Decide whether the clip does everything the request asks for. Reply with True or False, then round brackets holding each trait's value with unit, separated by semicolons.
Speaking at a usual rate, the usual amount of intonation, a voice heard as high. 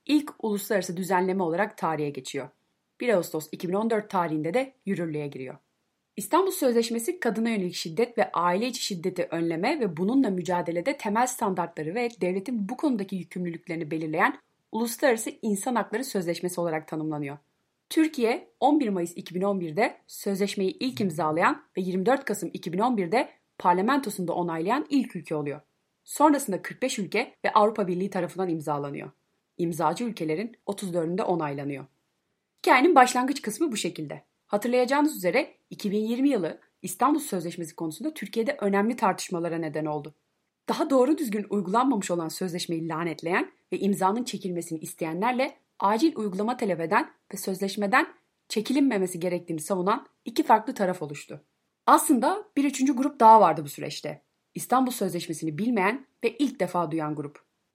False (130 wpm; 6.2 semitones; 200 Hz)